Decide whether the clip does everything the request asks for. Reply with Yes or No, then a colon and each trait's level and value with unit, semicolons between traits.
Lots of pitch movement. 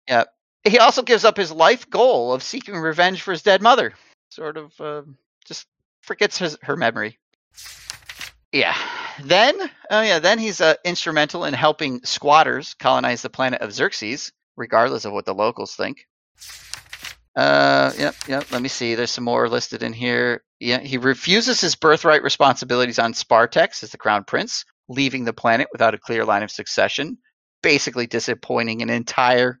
Yes: wide, 6.5 semitones